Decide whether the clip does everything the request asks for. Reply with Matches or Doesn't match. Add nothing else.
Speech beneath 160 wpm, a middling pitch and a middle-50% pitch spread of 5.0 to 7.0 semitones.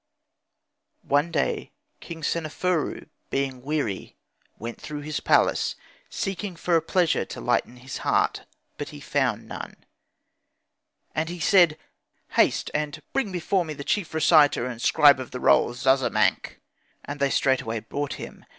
Doesn't match